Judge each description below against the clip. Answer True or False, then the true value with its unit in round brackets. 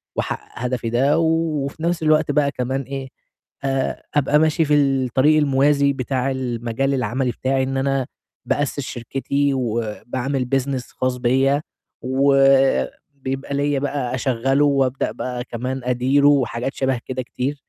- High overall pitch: False (135 Hz)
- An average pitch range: False (1.9 semitones)